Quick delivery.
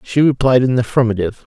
No: average, 195 wpm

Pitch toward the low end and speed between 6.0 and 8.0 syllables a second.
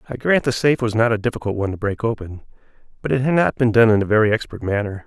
Yes: low, 115 Hz; 7.2 syllables/s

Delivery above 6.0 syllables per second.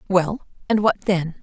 No: 4.5 syllables/s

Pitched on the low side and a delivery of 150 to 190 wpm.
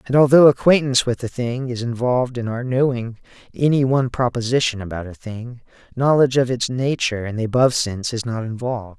Yes: low, 125 Hz; average, 185 wpm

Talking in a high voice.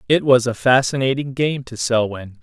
No: low, 125 Hz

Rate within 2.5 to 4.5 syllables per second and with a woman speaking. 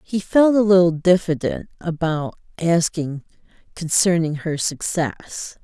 Yes: 3.9 syllables/s; female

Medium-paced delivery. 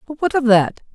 No: fast, 255 wpm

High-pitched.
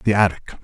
No: very low, 95 Hz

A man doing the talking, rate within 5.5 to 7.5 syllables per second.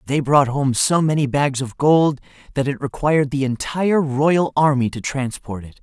No: male; 4.8 syllables/s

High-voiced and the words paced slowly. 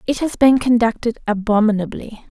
Yes: high, 230 Hz; slow, 125 wpm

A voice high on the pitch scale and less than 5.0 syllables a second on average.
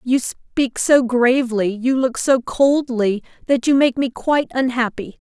Yes: very high, 250 Hz; 4.2 syllables/s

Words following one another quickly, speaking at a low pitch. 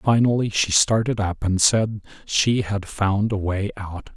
No: average, 175 wpm; low, 105 Hz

